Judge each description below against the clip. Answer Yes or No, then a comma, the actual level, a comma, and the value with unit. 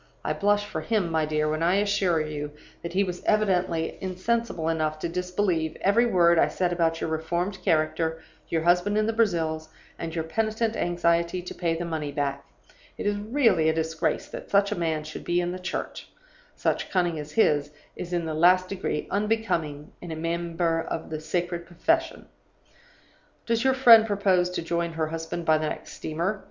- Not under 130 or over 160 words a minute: No, average, 190 wpm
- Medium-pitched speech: Yes, medium, 170 Hz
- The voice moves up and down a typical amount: Yes, average, 3.6 semitones